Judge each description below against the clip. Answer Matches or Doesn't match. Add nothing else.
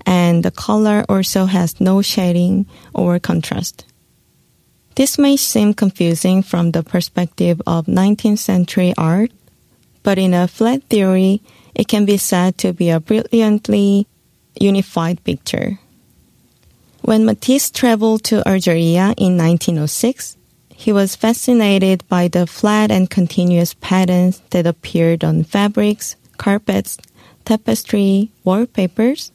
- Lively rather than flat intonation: Doesn't match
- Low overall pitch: Doesn't match